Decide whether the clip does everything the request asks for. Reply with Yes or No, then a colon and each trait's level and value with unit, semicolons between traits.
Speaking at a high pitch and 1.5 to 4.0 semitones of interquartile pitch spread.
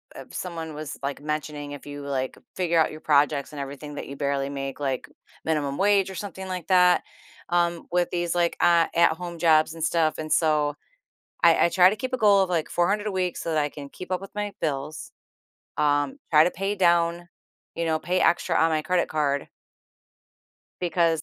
No: medium, 165 Hz; average, 3.3 semitones